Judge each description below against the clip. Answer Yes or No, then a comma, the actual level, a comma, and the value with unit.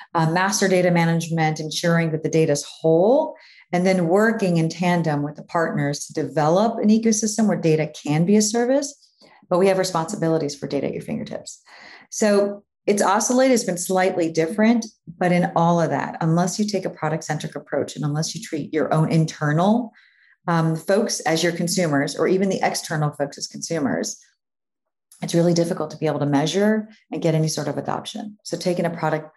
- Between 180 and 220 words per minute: Yes, average, 190 wpm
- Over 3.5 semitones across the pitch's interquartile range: Yes, average, 4.2 semitones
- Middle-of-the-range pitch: Yes, medium, 170 Hz